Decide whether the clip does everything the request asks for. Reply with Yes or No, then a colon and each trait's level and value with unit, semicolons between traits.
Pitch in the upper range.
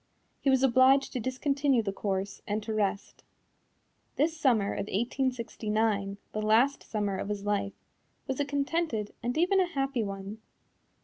Yes: high, 230 Hz